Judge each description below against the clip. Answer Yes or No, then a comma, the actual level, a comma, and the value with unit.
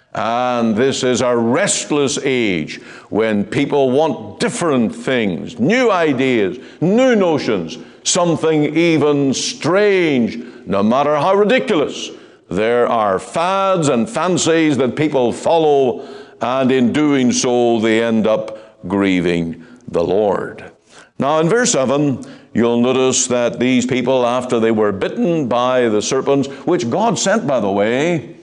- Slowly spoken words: Yes, slow, 130 wpm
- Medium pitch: No, low, 130 Hz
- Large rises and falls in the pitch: No, average, 4.1 semitones